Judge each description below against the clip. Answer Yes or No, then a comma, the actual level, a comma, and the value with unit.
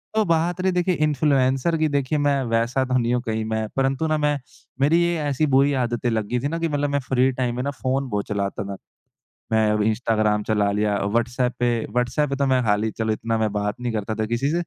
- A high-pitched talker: No, low, 125 Hz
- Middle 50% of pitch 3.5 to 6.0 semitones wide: Yes, average, 4.5 semitones